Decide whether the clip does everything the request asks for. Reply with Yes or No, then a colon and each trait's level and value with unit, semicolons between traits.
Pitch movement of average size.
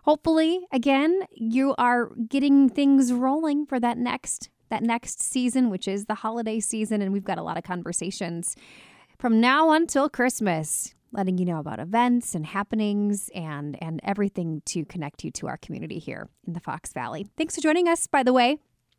No: wide, 6.0 semitones